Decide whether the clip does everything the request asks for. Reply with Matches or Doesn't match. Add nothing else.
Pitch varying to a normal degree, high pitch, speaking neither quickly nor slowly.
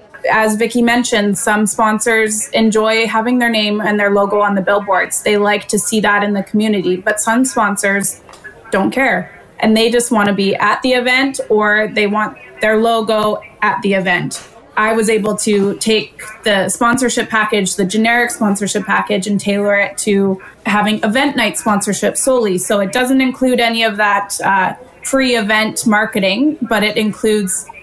Doesn't match